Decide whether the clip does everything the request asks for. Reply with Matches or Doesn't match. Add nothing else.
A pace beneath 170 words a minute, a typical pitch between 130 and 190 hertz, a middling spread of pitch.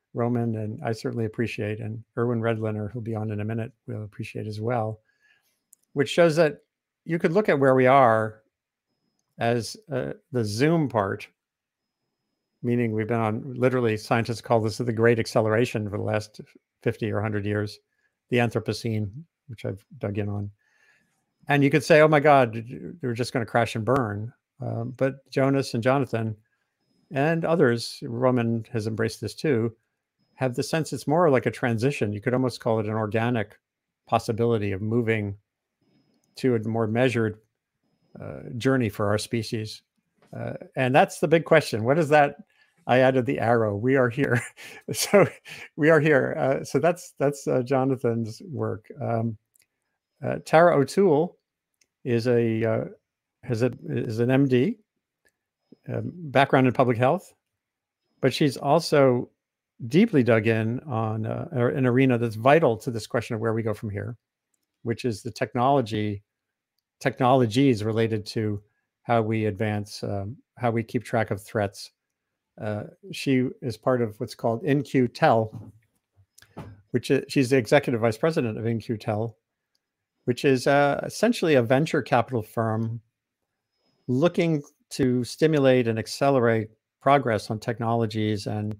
Doesn't match